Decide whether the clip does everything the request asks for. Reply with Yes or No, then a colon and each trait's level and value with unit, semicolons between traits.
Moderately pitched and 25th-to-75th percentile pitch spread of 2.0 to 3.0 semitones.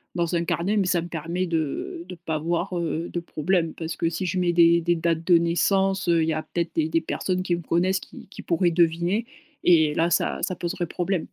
No: medium, 170 Hz; narrow, 1.6 semitones